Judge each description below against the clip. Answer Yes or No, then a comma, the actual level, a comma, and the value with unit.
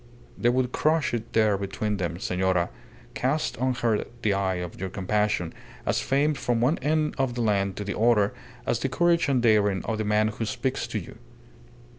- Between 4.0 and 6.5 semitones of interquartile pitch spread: Yes, average, 4.5 semitones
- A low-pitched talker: Yes, low, 110 Hz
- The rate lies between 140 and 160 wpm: No, average, 195 wpm